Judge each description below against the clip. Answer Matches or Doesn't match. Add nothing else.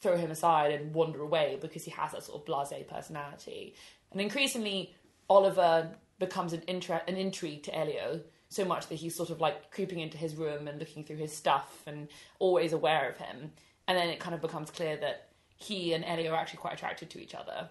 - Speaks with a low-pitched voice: Doesn't match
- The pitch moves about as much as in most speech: Matches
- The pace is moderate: Doesn't match